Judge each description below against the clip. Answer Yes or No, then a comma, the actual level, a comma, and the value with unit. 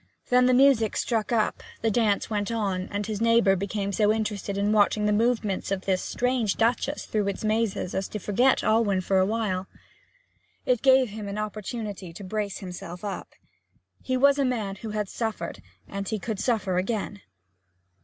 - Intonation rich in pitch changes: No, narrow, 2.6 semitones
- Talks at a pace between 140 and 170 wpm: No, average, 180 wpm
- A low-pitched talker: No, high, 210 Hz